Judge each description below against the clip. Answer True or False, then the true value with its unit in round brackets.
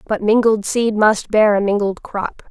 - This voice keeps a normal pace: True (190 wpm)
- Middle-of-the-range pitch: False (210 Hz)